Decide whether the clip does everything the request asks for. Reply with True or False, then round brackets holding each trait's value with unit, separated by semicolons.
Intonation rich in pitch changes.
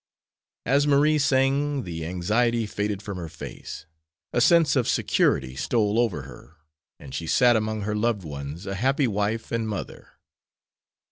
True (6.3 semitones)